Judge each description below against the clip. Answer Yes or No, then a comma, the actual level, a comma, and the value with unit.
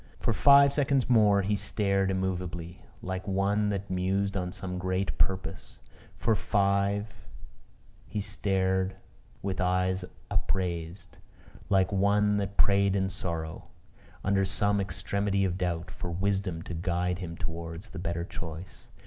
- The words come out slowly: Yes, slow, 130 wpm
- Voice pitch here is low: Yes, very low, 95 Hz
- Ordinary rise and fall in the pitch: No, narrow, 2.0 semitones